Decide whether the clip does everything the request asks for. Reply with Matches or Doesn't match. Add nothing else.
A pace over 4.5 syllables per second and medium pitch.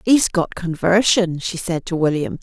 Doesn't match